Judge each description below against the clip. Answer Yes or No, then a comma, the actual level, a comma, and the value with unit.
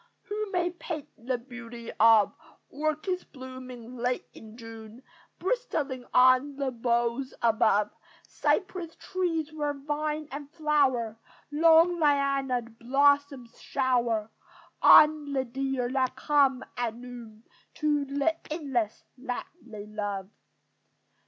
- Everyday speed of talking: No, slow, 110 wpm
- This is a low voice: No, very high, 265 Hz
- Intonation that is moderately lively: Yes, average, 4.1 semitones